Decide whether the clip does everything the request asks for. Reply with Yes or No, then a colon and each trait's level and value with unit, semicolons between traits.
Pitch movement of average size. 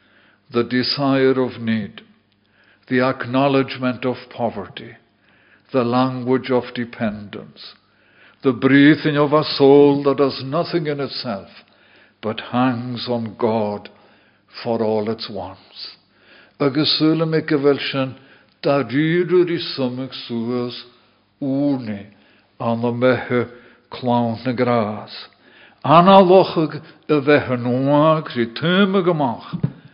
Yes: average, 3.6 semitones